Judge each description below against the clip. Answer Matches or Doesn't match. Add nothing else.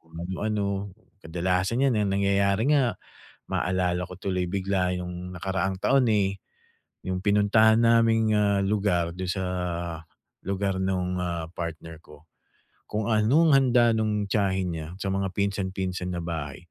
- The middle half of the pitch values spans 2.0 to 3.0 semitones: Matches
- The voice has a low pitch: Matches